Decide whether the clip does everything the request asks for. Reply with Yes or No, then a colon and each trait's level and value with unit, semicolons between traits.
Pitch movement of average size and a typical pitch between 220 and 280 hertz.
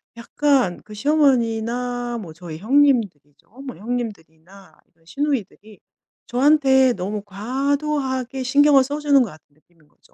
No: wide, 5.7 semitones; high, 245 Hz